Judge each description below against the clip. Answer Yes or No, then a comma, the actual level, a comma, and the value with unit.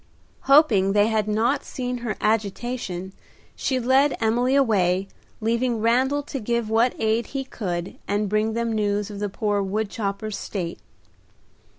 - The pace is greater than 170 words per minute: No, average, 150 wpm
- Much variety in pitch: No, average, 3.1 semitones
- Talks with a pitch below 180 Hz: No, high, 220 Hz